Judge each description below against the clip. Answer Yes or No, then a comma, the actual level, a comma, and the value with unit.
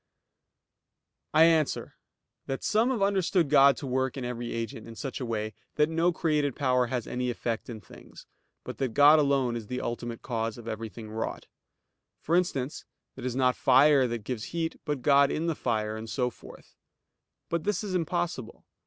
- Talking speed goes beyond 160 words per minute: Yes, average, 185 wpm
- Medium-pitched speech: No, low, 130 Hz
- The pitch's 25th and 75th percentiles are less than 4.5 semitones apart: No, average, 4.8 semitones